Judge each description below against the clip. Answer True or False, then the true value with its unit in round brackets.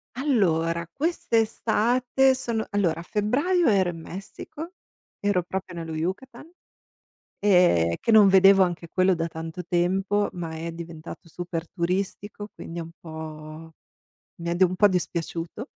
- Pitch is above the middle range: False (180 Hz)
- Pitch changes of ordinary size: True (3.8 semitones)